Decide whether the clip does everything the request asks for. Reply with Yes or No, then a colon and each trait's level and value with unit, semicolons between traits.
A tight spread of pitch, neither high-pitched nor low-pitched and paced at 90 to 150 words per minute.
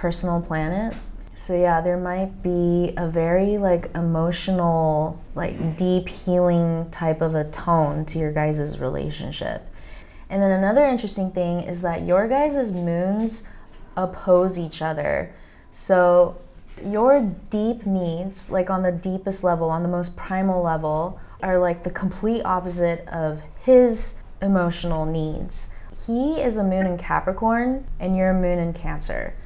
Yes: narrow, 2.3 semitones; medium, 180 Hz; average, 145 wpm